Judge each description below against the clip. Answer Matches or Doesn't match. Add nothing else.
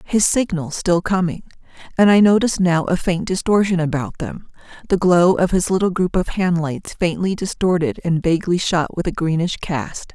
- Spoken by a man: Doesn't match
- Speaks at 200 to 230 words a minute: Doesn't match